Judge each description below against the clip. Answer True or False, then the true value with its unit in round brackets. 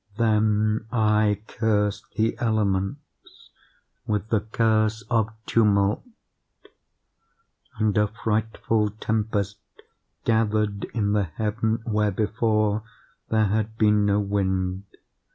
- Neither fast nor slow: False (100 wpm)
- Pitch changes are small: True (1.3 semitones)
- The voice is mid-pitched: False (105 Hz)